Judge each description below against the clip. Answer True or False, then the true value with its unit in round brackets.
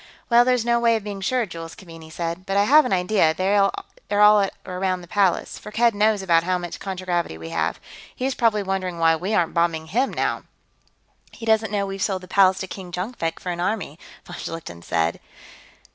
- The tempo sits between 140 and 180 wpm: False (205 wpm)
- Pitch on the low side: False (190 Hz)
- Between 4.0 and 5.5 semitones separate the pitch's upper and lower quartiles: False (3.6 semitones)